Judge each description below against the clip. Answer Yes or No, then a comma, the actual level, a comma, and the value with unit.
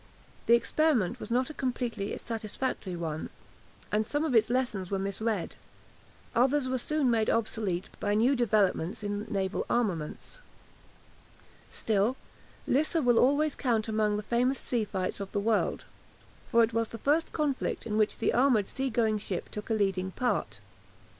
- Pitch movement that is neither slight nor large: Yes, average, 3.8 semitones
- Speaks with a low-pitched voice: No, high, 225 Hz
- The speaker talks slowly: No, average, 160 wpm